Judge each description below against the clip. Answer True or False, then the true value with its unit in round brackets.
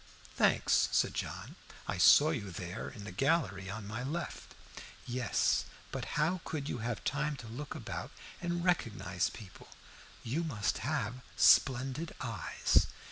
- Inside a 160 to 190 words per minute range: False (140 wpm)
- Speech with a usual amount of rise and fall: False (6.0 semitones)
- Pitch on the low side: True (125 Hz)